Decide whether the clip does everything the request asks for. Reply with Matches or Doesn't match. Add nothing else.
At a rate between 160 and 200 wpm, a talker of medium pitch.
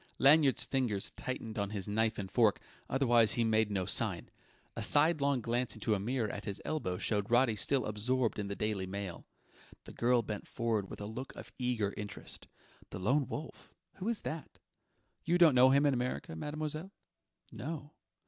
Doesn't match